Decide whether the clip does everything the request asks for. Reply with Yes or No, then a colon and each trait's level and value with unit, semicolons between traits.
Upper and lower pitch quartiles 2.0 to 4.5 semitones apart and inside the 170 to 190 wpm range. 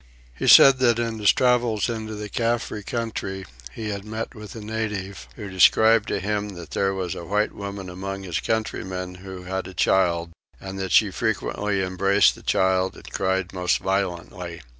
Yes: average, 2.8 semitones; average, 180 wpm